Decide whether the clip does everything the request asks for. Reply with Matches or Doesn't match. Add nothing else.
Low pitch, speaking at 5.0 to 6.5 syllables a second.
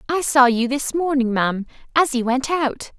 Doesn't match